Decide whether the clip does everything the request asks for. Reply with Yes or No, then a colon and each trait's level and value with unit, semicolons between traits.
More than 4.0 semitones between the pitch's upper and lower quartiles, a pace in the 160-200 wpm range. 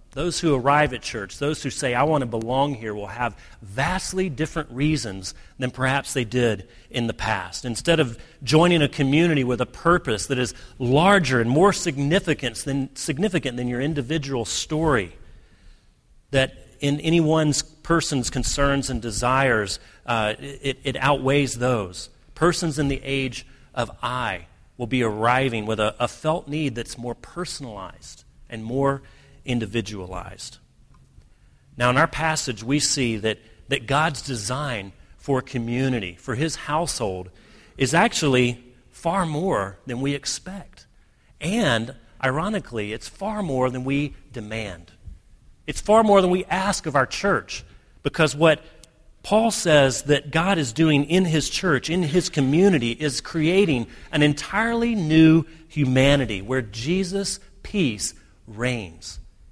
No: average, 5.0 semitones; average, 140 wpm